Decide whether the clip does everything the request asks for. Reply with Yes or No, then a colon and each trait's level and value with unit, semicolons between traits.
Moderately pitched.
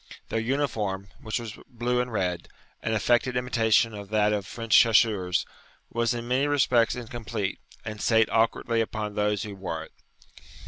No: low, 110 Hz